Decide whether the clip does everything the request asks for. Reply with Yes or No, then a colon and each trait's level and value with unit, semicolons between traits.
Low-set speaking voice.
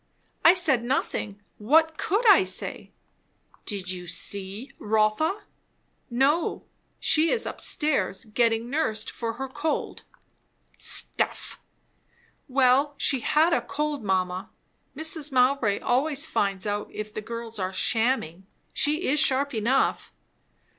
No: very high, 250 Hz